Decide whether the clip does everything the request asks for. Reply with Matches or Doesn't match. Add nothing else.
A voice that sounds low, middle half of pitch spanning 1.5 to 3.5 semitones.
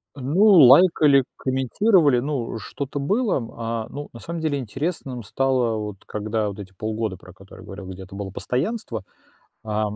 Doesn't match